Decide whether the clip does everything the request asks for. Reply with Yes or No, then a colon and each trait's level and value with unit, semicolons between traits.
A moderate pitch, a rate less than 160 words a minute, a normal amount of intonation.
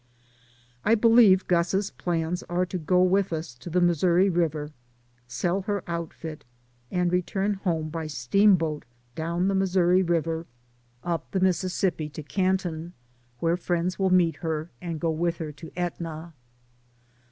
No: medium, 175 Hz; average, 150 wpm; narrow, 2.3 semitones